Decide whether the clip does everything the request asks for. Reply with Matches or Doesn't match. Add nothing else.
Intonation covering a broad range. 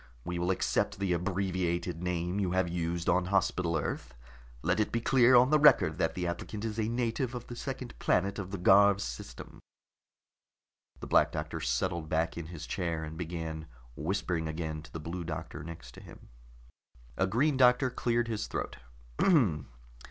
Doesn't match